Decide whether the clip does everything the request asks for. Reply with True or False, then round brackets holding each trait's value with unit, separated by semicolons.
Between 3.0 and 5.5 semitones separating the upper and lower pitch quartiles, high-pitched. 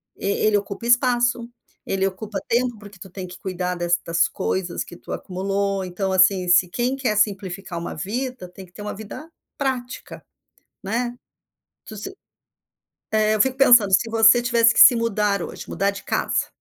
True (3.9 semitones; 205 Hz)